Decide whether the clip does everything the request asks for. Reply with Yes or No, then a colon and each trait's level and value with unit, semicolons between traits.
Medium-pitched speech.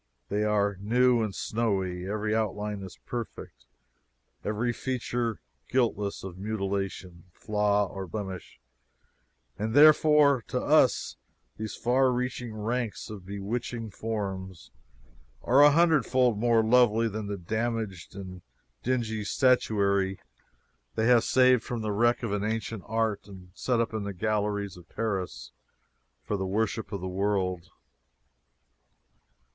No: low, 110 Hz